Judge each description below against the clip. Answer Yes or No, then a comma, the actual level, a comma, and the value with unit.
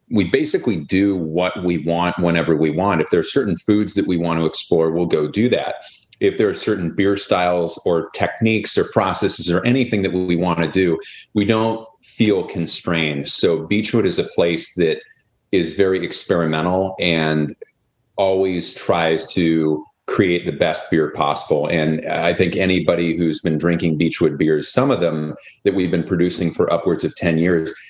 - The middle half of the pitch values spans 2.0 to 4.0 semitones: Yes, average, 3.3 semitones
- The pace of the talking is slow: No, average, 180 wpm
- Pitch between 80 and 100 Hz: Yes, very low, 85 Hz